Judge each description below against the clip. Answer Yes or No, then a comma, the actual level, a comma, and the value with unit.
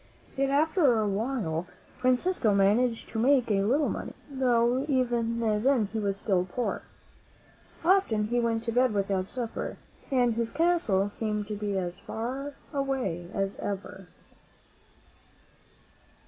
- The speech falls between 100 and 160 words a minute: Yes, slow, 135 wpm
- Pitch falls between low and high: No, high, 230 Hz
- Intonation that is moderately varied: Yes, average, 4.2 semitones